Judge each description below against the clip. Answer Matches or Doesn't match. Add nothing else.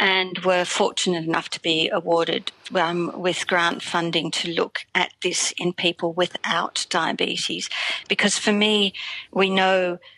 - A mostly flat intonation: Matches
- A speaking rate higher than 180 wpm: Doesn't match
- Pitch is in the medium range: Matches